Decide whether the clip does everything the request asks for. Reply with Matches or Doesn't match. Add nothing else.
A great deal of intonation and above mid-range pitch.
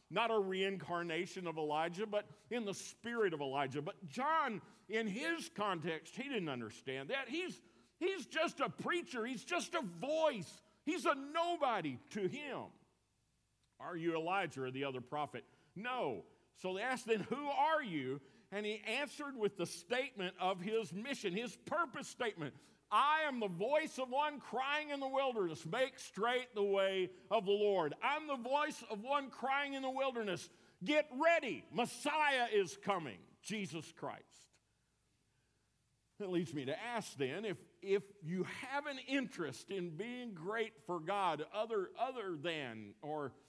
Matches